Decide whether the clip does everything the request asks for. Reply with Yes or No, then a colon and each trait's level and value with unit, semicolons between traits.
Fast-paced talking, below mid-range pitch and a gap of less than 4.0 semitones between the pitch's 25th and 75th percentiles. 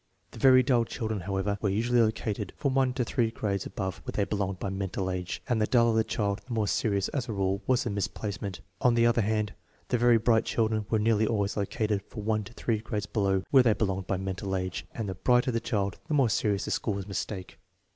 Yes: fast, 230 wpm; low, 105 Hz; average, 2.9 semitones